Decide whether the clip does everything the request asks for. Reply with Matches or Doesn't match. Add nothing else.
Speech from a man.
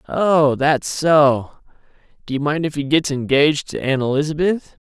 Matches